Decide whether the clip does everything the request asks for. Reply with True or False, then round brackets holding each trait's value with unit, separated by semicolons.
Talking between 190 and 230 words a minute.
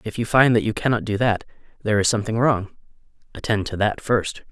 True (200 wpm)